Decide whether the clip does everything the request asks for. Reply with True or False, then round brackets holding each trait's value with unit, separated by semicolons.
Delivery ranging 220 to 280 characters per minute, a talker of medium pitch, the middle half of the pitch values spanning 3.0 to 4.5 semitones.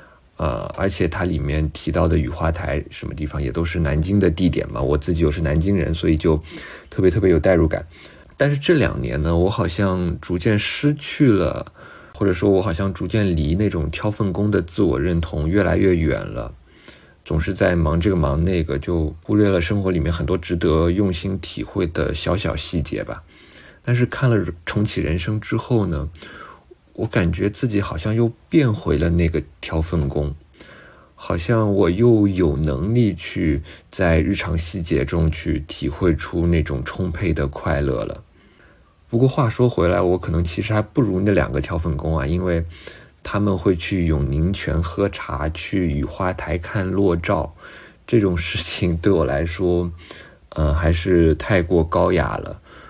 False (250 characters per minute; 85 Hz; 3.8 semitones)